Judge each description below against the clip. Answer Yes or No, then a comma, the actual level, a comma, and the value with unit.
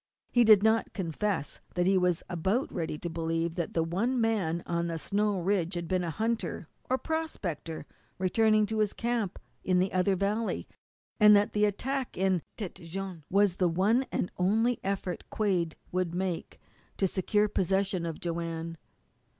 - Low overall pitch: No, high, 190 Hz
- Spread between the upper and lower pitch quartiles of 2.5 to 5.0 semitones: Yes, average, 3.7 semitones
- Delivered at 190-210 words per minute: No, average, 165 wpm